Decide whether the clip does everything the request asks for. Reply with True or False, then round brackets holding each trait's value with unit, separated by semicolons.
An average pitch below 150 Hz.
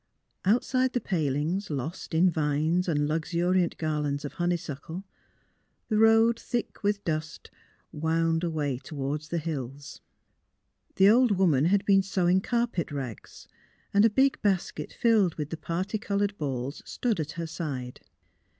False (170 Hz)